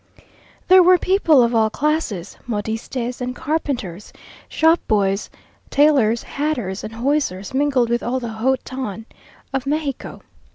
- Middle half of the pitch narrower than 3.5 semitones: No, average, 4.9 semitones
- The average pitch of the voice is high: Yes, very high, 250 Hz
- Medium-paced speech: No, slow, 130 wpm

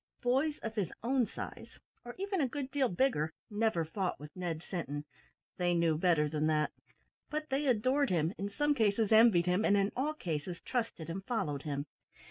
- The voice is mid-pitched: No, high, 200 Hz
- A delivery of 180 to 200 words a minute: Yes, average, 185 wpm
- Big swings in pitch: Yes, wide, 7.5 semitones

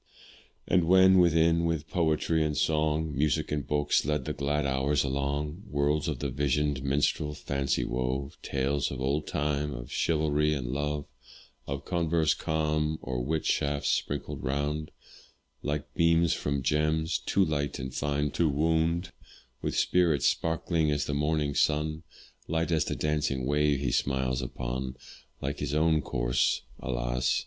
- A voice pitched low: Yes, very low, 75 Hz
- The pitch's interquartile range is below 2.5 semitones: Yes, narrow, 2.1 semitones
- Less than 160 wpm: Yes, average, 150 wpm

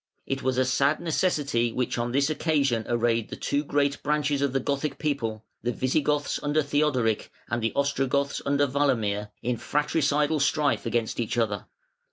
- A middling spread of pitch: Yes, average, 3.5 semitones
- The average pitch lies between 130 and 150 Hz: Yes, medium, 140 Hz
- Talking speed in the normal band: Yes, average, 170 wpm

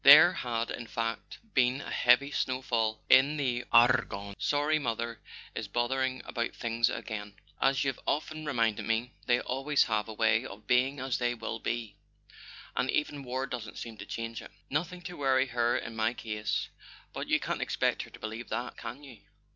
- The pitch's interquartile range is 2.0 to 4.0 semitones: Yes, average, 2.9 semitones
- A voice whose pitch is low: Yes, low, 120 Hz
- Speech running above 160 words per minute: Yes, average, 185 wpm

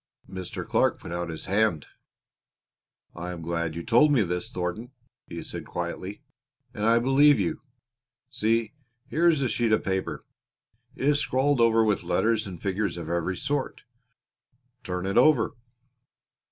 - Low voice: Yes, low, 105 Hz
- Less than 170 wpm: Yes, average, 155 wpm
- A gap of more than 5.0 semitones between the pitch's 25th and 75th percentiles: Yes, wide, 5.6 semitones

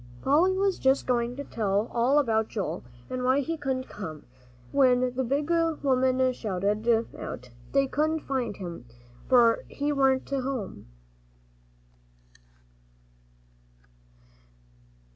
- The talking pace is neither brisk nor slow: No, slow, 115 wpm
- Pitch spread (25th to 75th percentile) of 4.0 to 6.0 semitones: No, average, 3.6 semitones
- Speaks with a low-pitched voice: No, very high, 255 Hz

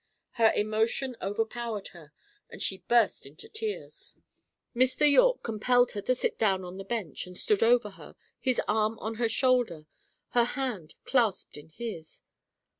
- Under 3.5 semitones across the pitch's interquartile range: No, average, 4.1 semitones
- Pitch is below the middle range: No, high, 225 Hz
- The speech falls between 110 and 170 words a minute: Yes, average, 155 wpm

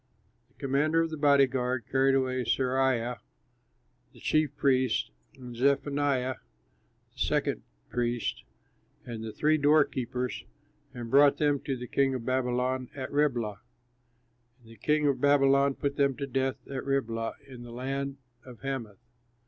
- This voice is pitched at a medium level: No, low, 130 Hz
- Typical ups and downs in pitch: No, narrow, 2.1 semitones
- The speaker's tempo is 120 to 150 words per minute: Yes, average, 145 wpm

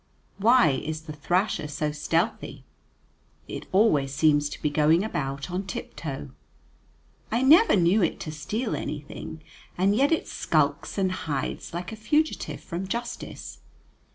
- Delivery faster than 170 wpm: No, average, 145 wpm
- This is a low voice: No, medium, 170 Hz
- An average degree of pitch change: No, wide, 6.3 semitones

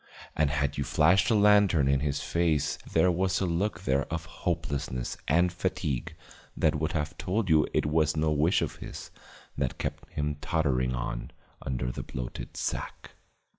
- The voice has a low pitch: Yes, very low, 75 Hz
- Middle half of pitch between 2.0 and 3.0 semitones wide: No, average, 3.8 semitones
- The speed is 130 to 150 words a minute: No, average, 170 wpm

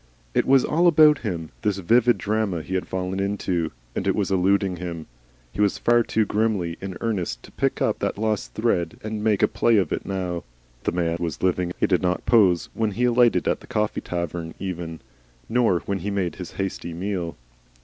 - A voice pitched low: Yes, very low, 95 Hz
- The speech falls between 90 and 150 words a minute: No, average, 200 wpm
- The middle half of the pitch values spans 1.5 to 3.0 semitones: No, average, 3.8 semitones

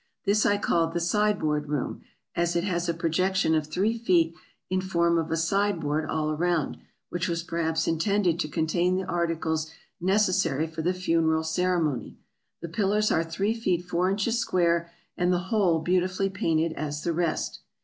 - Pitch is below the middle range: No, medium, 170 Hz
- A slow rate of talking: No, average, 170 wpm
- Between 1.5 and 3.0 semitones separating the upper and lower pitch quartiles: Yes, narrow, 2.6 semitones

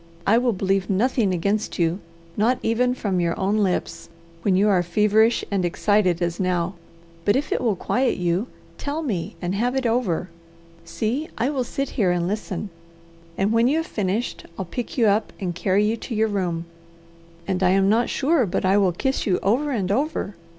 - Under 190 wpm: No, average, 195 wpm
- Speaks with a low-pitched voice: No, high, 205 Hz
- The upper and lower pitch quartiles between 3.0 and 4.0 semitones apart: No, average, 4.4 semitones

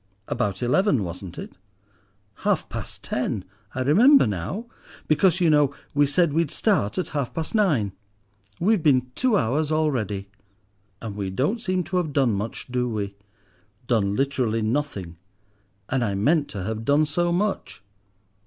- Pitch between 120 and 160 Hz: Yes, medium, 140 Hz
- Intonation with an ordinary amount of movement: No, wide, 7.4 semitones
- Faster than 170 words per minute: No, average, 155 wpm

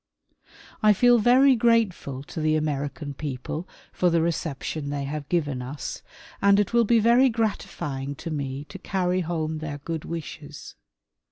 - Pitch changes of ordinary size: No, wide, 6.1 semitones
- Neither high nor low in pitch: Yes, medium, 160 Hz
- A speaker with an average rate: Yes, average, 155 wpm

